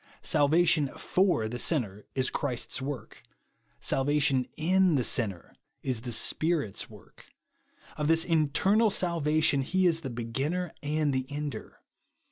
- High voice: No, medium, 145 Hz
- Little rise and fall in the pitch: No, average, 4.2 semitones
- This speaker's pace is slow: Yes, slow, 125 wpm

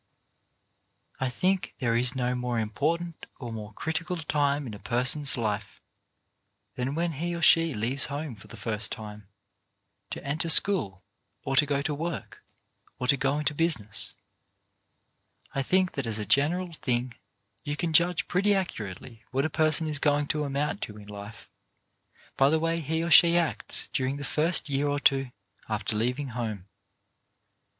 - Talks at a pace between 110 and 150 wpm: No, average, 165 wpm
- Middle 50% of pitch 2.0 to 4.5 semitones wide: No, average, 5.3 semitones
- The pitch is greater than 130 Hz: Yes, medium, 140 Hz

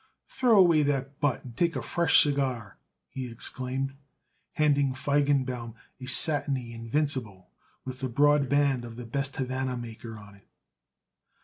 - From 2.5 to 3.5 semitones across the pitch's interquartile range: Yes, average, 3.2 semitones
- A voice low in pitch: Yes, low, 130 Hz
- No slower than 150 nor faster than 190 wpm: No, average, 140 wpm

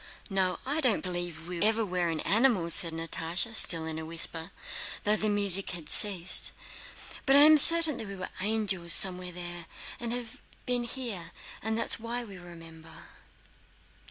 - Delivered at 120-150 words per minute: No, average, 170 wpm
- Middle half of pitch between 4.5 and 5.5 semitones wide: Yes, average, 5.0 semitones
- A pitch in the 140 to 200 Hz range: Yes, medium, 185 Hz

